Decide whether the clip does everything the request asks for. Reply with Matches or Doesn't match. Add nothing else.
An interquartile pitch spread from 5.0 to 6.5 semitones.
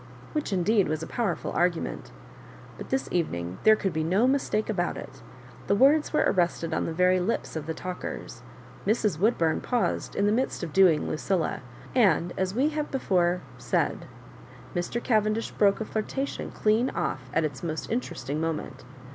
Matches